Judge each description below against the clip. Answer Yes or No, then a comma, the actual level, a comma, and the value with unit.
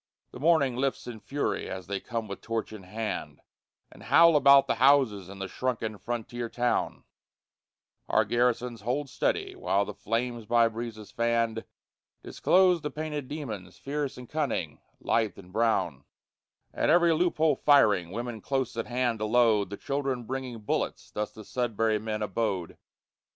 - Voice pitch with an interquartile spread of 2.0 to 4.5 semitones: Yes, average, 4.0 semitones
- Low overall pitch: Yes, low, 115 Hz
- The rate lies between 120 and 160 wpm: Yes, average, 155 wpm